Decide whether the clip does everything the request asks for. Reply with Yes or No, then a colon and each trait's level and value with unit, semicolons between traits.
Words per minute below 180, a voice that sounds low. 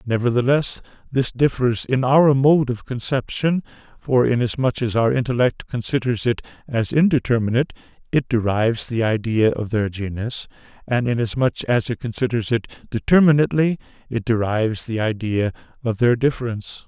Yes: slow, 135 wpm; low, 120 Hz